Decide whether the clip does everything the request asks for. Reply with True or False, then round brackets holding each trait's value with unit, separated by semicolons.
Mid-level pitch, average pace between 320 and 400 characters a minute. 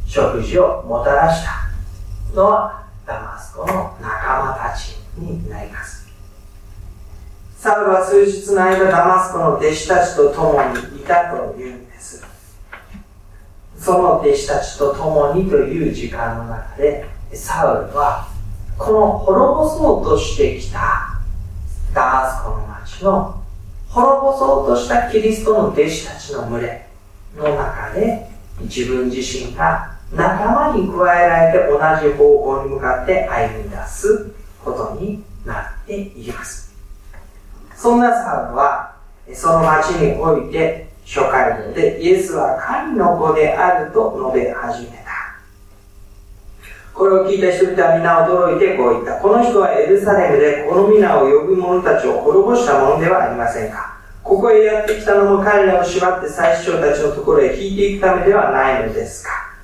False (155 Hz; 275 characters per minute)